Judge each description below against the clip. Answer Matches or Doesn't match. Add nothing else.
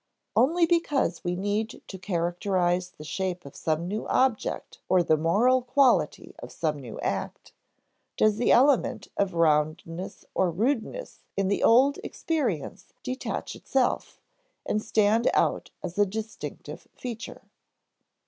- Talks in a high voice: Matches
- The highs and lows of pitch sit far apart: Matches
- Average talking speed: Doesn't match